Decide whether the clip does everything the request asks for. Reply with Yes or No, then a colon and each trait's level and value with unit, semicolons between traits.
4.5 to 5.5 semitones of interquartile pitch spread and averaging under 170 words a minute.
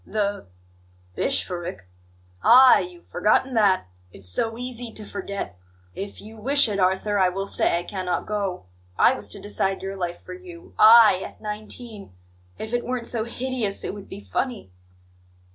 No: average, 4.0 semitones; average, 160 wpm